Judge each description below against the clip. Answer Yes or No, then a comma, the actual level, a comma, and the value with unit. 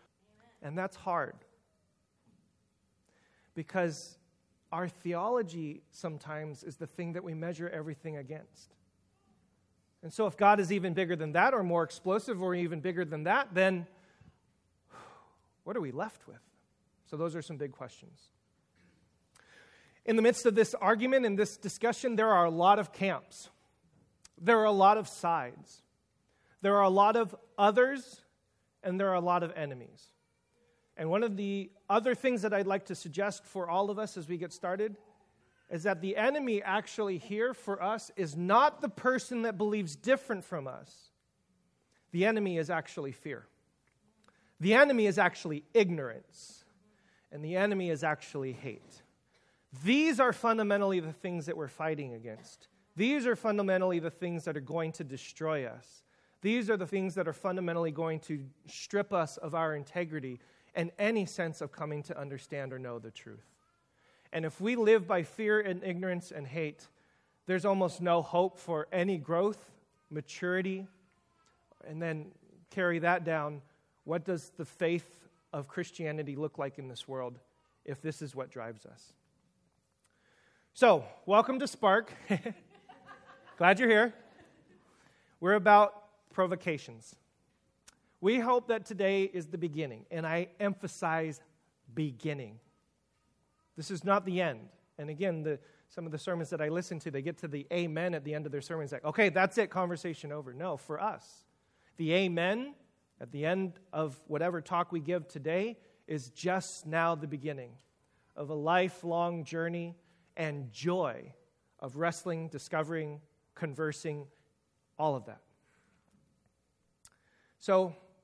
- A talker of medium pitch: Yes, medium, 175 Hz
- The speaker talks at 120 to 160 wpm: Yes, average, 155 wpm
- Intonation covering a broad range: No, average, 4.2 semitones